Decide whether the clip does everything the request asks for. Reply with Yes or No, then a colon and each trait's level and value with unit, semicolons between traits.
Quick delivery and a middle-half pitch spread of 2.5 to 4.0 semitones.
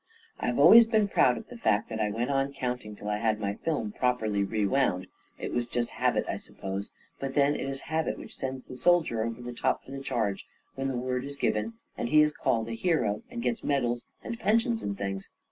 No: fast, 230 wpm; average, 4.7 semitones